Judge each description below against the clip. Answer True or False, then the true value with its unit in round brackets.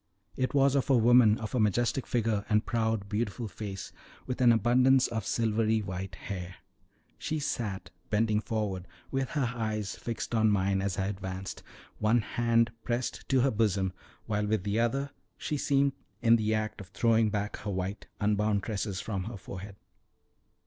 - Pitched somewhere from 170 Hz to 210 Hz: False (110 Hz)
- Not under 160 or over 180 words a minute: True (170 wpm)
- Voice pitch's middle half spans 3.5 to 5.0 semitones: False (2.8 semitones)